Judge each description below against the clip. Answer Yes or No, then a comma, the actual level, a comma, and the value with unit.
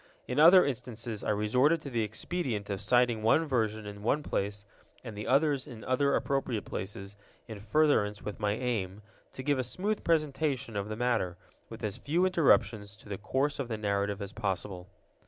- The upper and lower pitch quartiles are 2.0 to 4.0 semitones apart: No, average, 5.1 semitones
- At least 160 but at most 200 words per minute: Yes, average, 185 wpm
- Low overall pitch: Yes, low, 115 Hz